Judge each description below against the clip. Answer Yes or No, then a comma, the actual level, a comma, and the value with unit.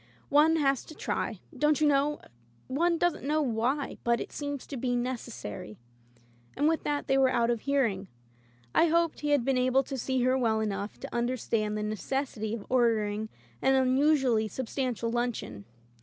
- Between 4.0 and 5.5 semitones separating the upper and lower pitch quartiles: Yes, average, 4.4 semitones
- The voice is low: No, very high, 255 Hz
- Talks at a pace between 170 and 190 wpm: Yes, average, 185 wpm